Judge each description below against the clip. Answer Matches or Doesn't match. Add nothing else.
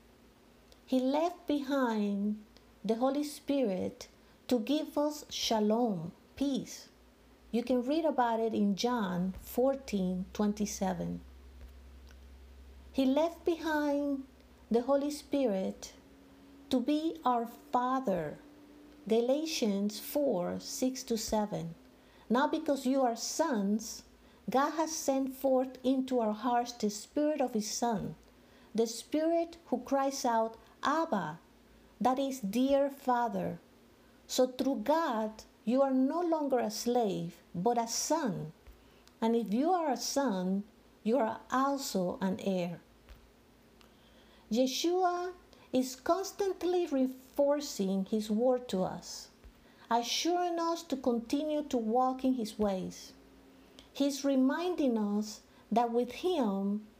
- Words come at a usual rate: Doesn't match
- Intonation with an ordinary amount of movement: Matches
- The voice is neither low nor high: Doesn't match